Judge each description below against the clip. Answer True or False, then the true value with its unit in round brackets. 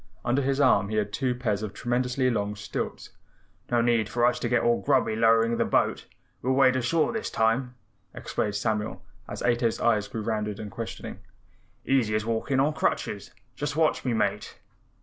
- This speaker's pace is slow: False (180 wpm)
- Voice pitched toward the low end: True (120 Hz)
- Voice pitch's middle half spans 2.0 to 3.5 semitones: True (2.9 semitones)